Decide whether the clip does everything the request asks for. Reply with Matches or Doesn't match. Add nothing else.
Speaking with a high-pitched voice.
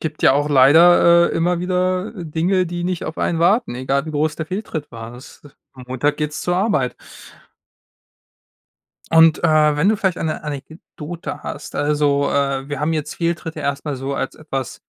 Doesn't match